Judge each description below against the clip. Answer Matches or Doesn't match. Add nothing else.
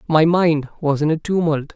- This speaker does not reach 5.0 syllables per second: Matches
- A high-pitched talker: Doesn't match